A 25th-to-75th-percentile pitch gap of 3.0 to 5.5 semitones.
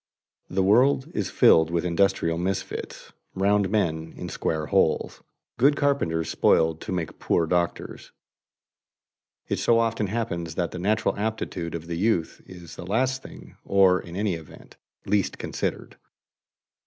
Yes: average, 4.4 semitones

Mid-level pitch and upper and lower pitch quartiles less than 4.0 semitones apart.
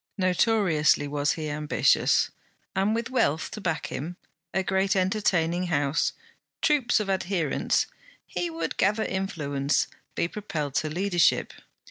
No: medium, 175 Hz; average, 4.4 semitones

